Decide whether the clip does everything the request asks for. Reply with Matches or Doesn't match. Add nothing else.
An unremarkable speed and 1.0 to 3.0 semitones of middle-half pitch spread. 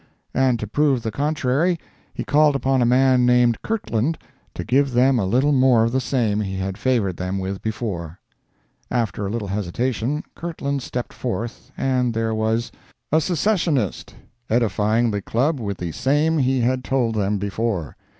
Doesn't match